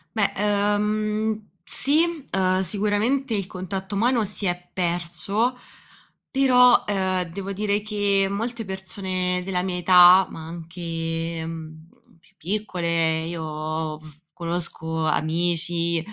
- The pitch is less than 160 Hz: No, medium, 185 Hz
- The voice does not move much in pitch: No, average, 3.7 semitones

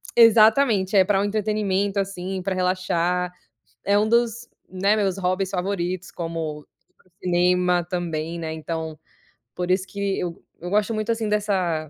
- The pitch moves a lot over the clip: No, average, 2.7 semitones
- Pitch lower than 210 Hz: Yes, medium, 185 Hz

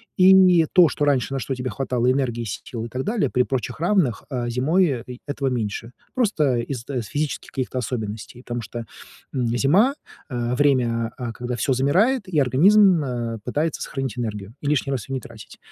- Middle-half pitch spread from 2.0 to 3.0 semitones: No, average, 3.9 semitones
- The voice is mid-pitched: No, low, 130 Hz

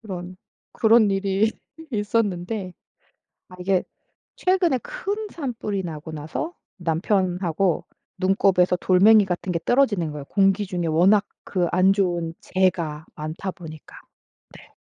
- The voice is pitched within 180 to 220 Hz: Yes, high, 190 Hz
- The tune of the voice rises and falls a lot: No, average, 3.3 semitones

